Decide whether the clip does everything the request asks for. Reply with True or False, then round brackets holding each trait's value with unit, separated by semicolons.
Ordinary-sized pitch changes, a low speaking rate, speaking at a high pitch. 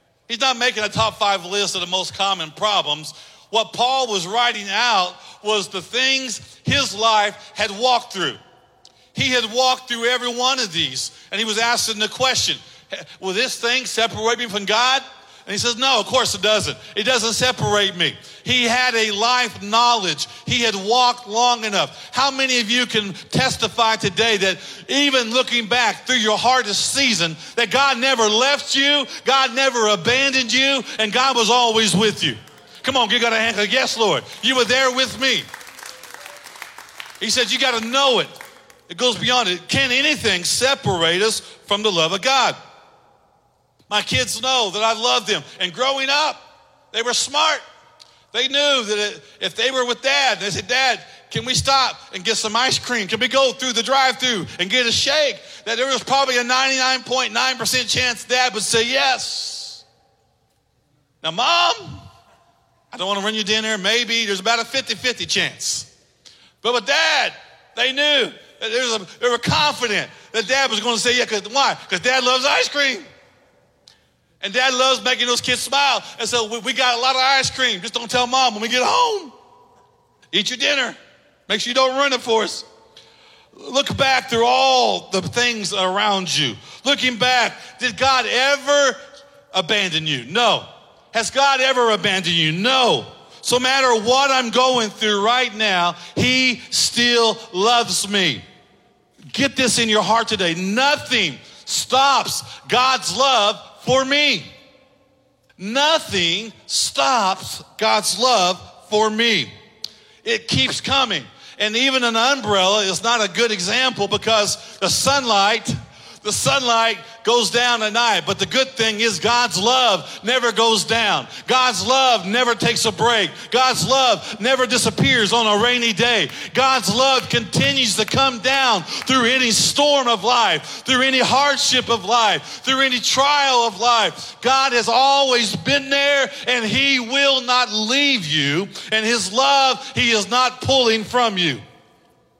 False (3.4 semitones; 170 wpm; 240 Hz)